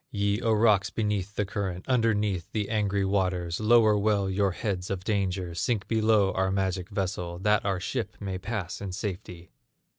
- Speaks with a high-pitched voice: No, low, 100 Hz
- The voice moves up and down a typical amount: No, narrow, 2.3 semitones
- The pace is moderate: Yes, average, 170 wpm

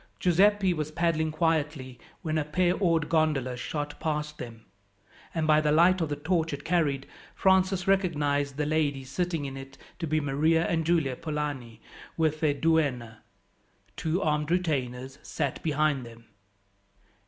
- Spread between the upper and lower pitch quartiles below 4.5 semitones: Yes, average, 2.8 semitones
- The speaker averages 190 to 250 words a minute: No, average, 150 wpm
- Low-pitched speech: No, medium, 155 Hz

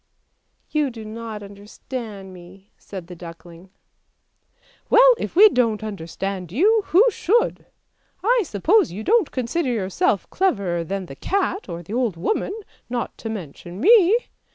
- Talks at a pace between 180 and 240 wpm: No, average, 155 wpm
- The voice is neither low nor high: No, high, 220 Hz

